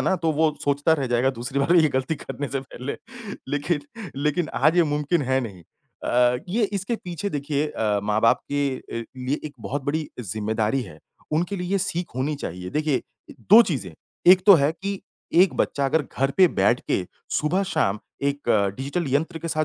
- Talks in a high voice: No, medium, 145 Hz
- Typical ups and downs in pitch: Yes, average, 4.6 semitones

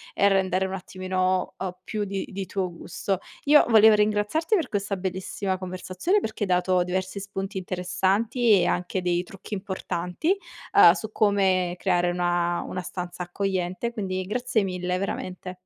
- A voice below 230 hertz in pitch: Yes, high, 190 Hz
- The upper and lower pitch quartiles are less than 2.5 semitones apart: Yes, narrow, 2.0 semitones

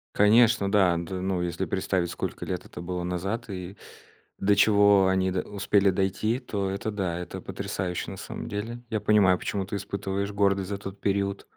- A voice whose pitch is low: Yes, low, 100 Hz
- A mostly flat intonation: Yes, narrow, 1.7 semitones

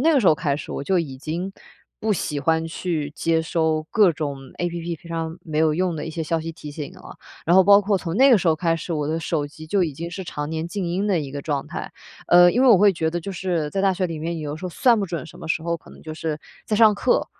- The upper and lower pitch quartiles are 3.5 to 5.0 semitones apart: No, average, 3.0 semitones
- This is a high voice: No, medium, 165 Hz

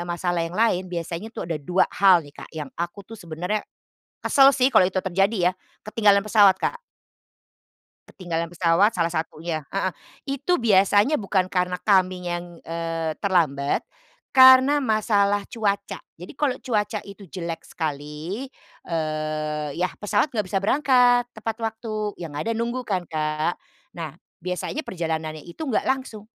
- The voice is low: No, medium, 185 Hz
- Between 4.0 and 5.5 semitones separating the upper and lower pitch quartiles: Yes, average, 4.4 semitones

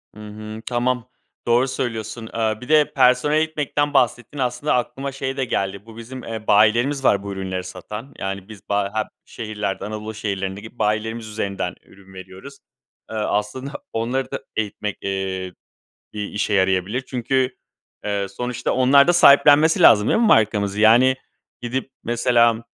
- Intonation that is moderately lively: Yes, average, 3.9 semitones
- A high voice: No, low, 110 Hz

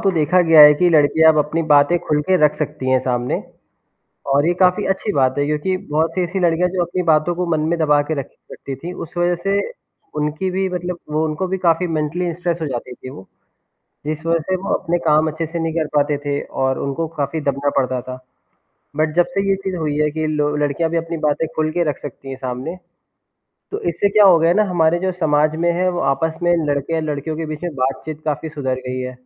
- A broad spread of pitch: No, average, 3.0 semitones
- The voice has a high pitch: No, medium, 155 Hz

